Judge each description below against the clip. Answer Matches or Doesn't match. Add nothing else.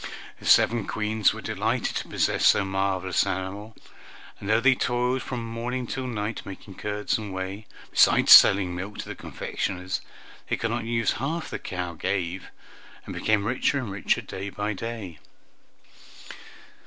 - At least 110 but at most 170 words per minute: Matches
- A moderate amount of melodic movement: Matches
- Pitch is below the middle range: Matches